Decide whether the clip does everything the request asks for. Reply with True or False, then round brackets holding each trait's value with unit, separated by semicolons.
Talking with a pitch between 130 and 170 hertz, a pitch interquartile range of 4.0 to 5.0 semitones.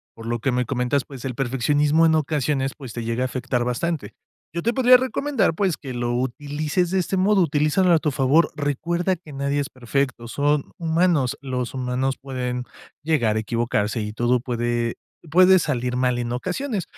True (135 Hz; 4.7 semitones)